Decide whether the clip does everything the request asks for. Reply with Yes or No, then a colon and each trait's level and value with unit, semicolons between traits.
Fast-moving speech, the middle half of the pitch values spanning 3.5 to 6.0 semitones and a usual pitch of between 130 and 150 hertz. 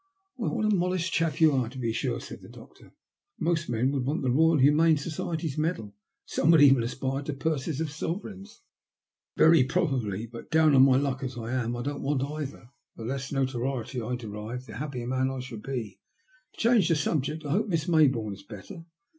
Yes: fast, 215 wpm; average, 4.5 semitones; low, 135 Hz